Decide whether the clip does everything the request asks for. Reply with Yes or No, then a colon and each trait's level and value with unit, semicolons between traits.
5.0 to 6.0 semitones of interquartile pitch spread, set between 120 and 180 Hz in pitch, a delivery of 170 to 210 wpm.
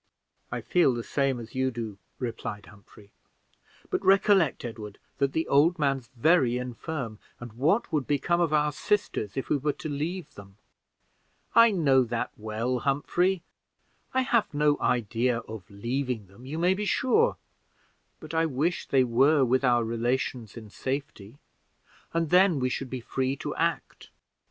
No: wide, 5.4 semitones; low, 135 Hz; average, 160 wpm